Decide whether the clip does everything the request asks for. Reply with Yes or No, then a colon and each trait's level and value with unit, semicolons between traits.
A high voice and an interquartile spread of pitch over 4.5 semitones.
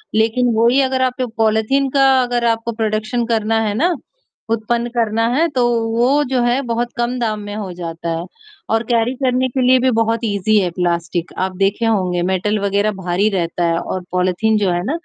No: high, 225 Hz; average, 3.8 semitones